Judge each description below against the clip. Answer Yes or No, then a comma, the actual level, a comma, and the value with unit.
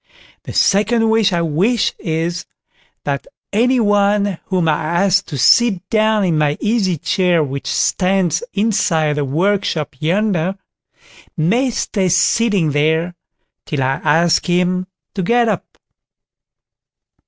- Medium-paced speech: No, slow, 125 wpm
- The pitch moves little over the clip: No, average, 4.5 semitones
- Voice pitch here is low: No, medium, 185 Hz